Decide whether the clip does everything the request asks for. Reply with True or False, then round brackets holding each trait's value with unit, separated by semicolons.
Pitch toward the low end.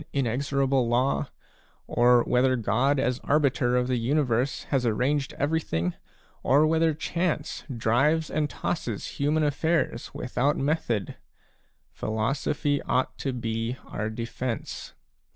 True (130 Hz)